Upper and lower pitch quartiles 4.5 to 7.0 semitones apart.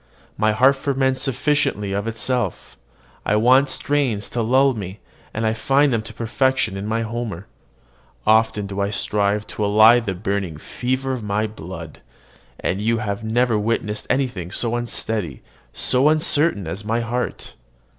No: average, 3.7 semitones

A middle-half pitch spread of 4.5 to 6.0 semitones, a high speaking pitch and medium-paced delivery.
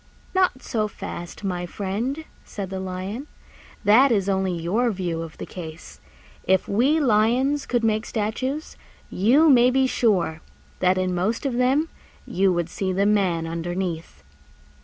Yes: average, 5.3 semitones; high, 200 Hz; average, 150 wpm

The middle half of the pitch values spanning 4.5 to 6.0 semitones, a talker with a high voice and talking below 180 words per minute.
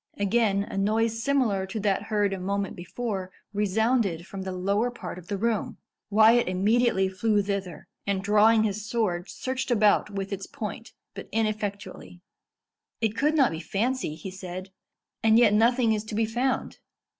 No: average, 2.8 semitones; high, 210 Hz; average, 165 wpm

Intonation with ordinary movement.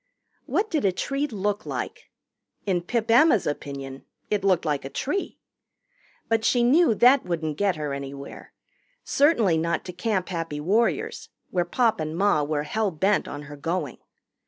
No: wide, 7.0 semitones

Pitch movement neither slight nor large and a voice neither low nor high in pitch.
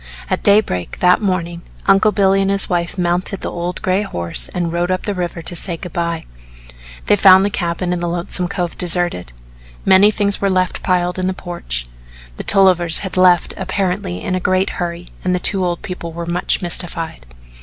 No: narrow, 1.7 semitones; medium, 180 Hz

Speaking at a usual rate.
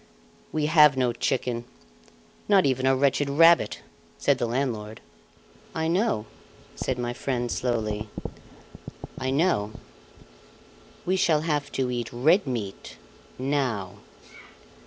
No: slow, 115 wpm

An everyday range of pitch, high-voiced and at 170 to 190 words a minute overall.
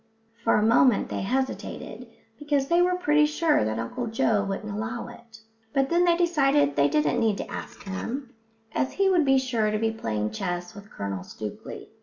No: wide, 6.5 semitones; high, 230 Hz; average, 185 wpm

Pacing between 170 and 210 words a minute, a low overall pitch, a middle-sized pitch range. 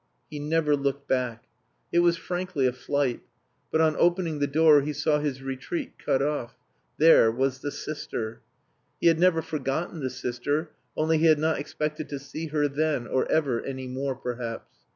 No: average, 175 wpm; medium, 145 Hz; average, 3.1 semitones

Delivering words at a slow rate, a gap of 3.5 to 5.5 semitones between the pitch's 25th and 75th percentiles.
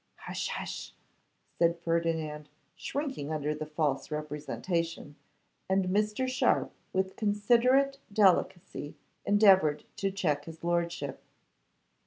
Yes: slow, 100 wpm; average, 5.1 semitones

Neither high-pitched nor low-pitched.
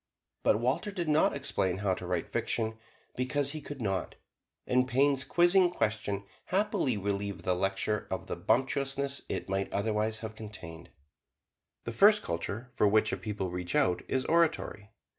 No: low, 110 Hz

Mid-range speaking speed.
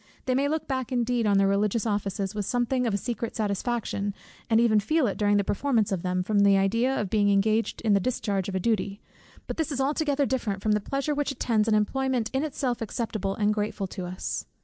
No: fast, 225 wpm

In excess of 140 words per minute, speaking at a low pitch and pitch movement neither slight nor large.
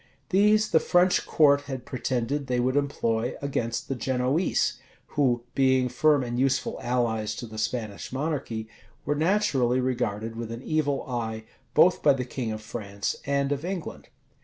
Yes: average, 160 wpm; low, 130 Hz; average, 3.5 semitones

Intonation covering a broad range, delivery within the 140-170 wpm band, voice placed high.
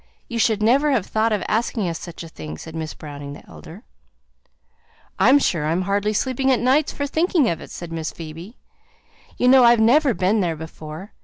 No: wide, 7.4 semitones; average, 200 wpm; high, 210 Hz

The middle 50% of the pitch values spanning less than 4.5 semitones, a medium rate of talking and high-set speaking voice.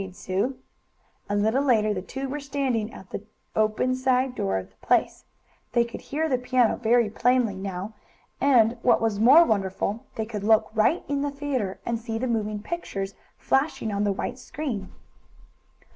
Yes: average, 3.9 semitones; average, 185 wpm; high, 230 Hz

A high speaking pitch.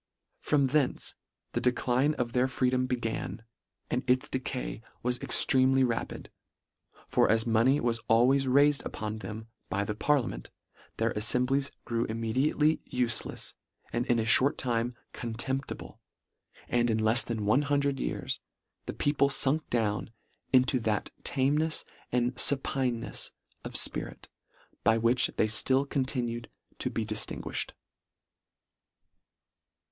No: low, 125 Hz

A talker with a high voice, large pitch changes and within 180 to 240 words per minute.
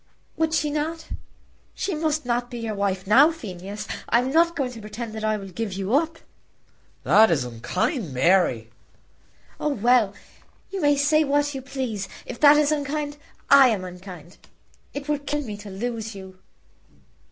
No: high, 240 Hz; wide, 6.8 semitones; average, 170 wpm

